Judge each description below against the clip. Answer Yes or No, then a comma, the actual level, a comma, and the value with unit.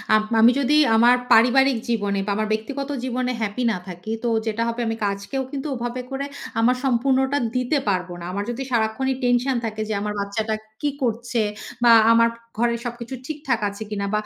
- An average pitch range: Yes, average, 3.1 semitones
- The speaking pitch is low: No, high, 235 Hz